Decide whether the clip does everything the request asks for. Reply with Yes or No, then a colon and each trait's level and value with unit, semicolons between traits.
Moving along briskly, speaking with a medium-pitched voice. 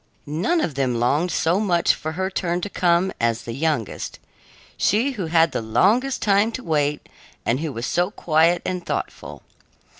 No: average, 175 wpm; medium, 170 Hz